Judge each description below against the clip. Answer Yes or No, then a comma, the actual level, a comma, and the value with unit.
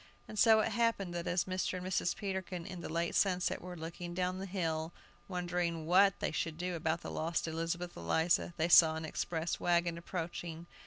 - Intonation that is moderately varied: No, narrow, 1.7 semitones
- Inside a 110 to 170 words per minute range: No, average, 195 wpm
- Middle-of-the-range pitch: Yes, medium, 175 Hz